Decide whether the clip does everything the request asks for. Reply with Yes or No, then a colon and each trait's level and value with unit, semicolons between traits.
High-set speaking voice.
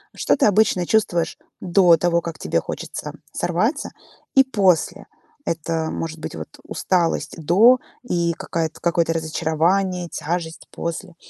No: medium, 170 Hz